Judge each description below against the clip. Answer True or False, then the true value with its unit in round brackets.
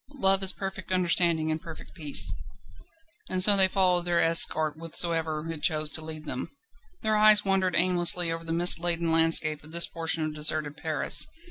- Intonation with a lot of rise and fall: False (2.7 semitones)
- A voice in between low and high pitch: True (165 Hz)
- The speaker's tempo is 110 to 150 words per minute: False (175 wpm)